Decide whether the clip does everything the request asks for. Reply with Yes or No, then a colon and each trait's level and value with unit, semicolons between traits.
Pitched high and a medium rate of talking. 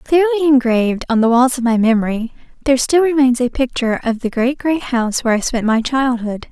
No: very high, 250 Hz; fast, 210 wpm